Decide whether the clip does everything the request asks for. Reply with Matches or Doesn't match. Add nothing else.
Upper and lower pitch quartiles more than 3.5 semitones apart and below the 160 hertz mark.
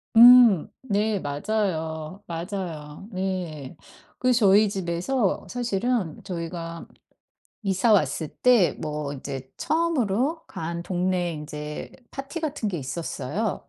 Doesn't match